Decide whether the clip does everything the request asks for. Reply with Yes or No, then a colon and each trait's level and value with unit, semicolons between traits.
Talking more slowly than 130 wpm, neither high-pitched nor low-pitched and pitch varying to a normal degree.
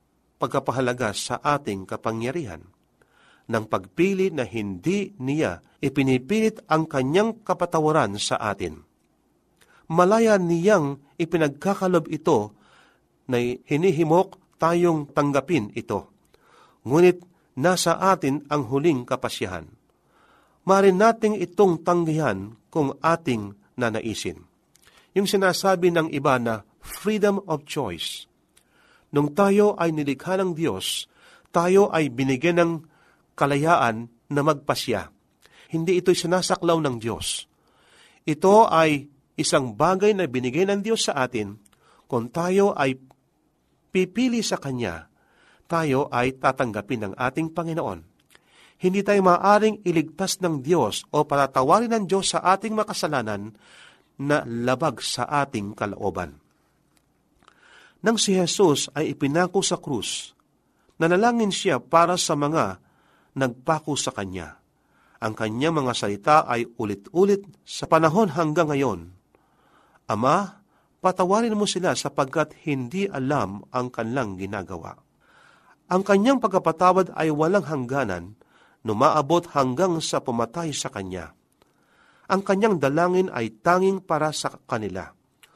No: slow, 110 wpm; medium, 155 Hz; wide, 6.4 semitones